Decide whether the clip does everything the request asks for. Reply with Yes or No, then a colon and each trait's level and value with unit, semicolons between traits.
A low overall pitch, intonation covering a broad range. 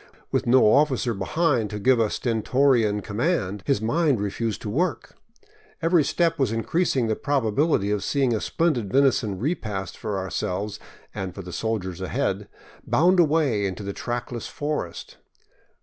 Yes: low, 115 Hz; wide, 5.8 semitones